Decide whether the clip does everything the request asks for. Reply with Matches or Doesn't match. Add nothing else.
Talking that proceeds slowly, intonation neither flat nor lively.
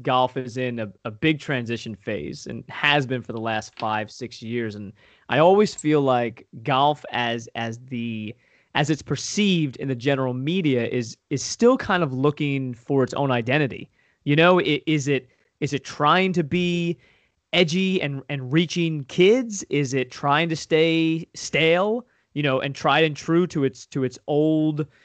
Doesn't match